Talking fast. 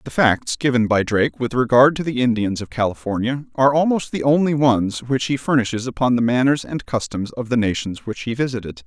Yes: fast, 210 wpm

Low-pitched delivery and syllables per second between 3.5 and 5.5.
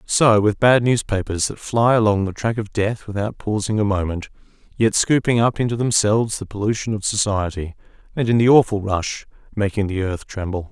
Yes: low, 105 Hz; 5.3 syllables/s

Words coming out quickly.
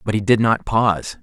Yes: fast, 245 wpm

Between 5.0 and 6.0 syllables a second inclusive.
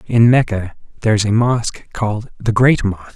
No: 4.8 syllables/s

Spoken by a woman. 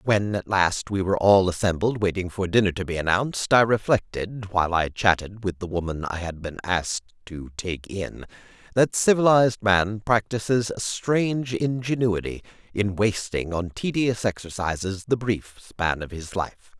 No: male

